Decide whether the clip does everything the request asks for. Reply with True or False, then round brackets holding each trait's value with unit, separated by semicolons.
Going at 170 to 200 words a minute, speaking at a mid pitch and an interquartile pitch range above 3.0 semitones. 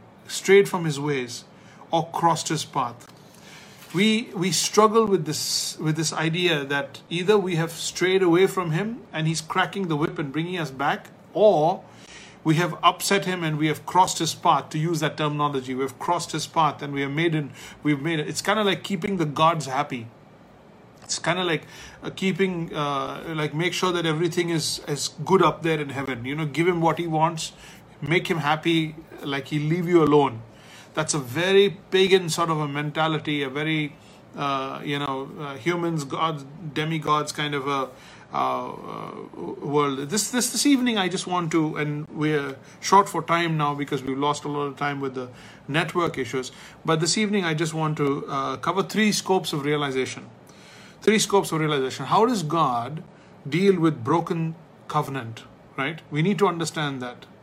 True (190 wpm; 160 Hz; 3.5 semitones)